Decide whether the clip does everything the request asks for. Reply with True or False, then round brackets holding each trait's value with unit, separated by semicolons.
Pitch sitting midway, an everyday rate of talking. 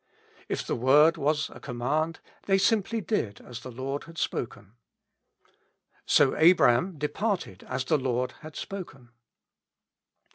False (145 Hz; 130 wpm)